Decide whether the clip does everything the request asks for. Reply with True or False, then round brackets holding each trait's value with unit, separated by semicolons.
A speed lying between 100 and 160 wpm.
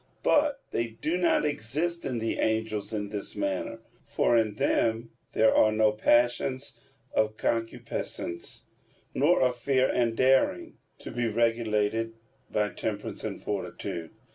True (135 wpm)